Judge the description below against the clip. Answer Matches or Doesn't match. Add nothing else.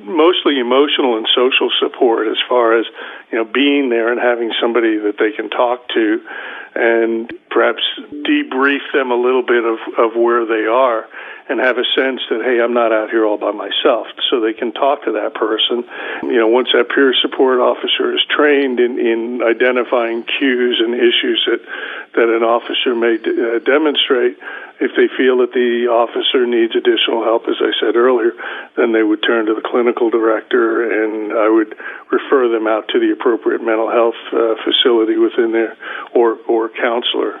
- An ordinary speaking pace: Matches